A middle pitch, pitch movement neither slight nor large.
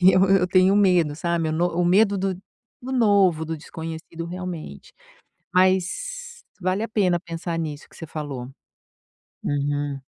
Yes: medium, 175 Hz; average, 3.0 semitones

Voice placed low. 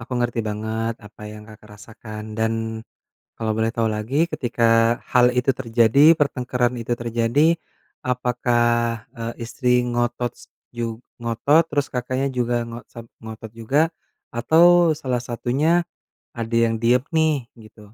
Yes: low, 120 Hz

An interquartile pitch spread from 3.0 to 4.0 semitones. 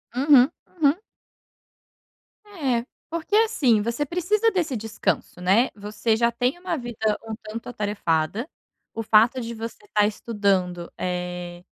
No: wide, 5.5 semitones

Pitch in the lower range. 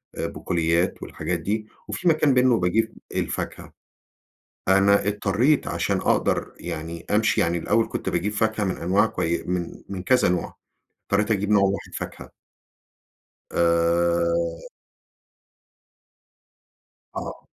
Yes: very low, 95 Hz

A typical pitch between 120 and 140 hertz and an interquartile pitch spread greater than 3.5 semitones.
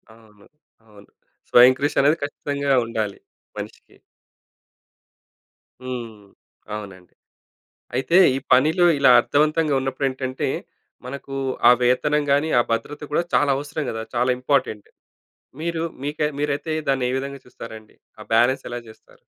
Yes: low, 135 Hz; average, 4.0 semitones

